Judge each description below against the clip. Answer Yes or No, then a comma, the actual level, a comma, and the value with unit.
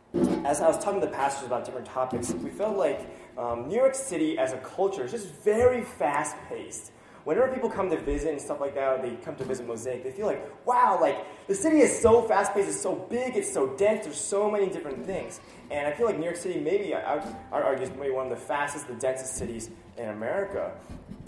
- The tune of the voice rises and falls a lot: Yes, wide, 8.3 semitones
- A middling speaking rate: No, fast, 230 wpm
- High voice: No, medium, 160 Hz